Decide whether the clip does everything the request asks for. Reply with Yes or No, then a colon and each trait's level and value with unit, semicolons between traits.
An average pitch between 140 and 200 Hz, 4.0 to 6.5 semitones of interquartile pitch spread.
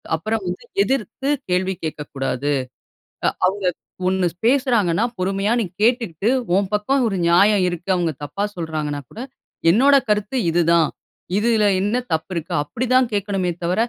Yes: high, 195 Hz; average, 4.4 semitones